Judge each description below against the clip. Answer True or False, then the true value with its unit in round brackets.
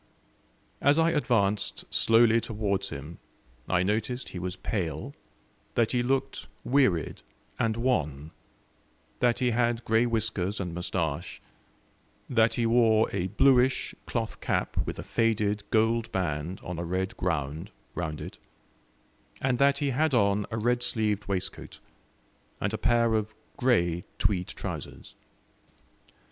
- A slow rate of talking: True (130 wpm)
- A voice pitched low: True (110 Hz)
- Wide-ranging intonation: False (4.6 semitones)